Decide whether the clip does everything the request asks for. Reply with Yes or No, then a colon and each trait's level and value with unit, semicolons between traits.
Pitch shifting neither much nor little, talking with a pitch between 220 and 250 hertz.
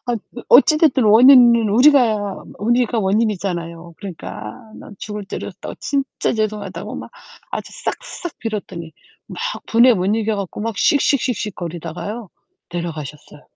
No: average, 4.7 semitones; high, 210 Hz